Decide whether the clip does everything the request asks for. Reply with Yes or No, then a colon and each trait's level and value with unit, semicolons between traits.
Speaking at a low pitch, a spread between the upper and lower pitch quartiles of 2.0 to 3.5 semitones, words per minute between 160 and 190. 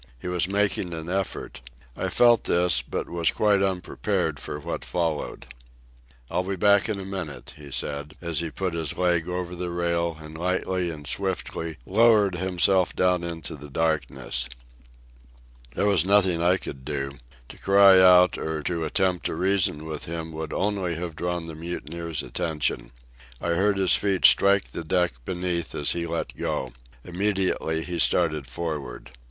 Yes: very low, 85 Hz; average, 2.8 semitones; average, 165 wpm